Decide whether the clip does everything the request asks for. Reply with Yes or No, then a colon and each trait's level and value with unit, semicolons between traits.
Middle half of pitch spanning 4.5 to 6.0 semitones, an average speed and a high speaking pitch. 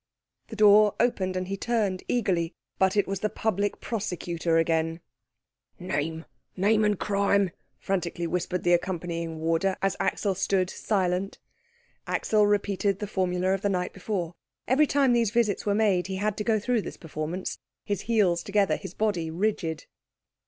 No: average, 2.9 semitones; average, 160 wpm; high, 195 Hz